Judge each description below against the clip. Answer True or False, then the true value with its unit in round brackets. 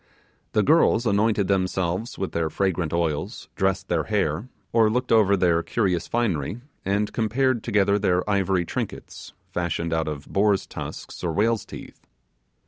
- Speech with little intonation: False (4.1 semitones)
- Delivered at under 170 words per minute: True (145 wpm)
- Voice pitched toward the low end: True (100 Hz)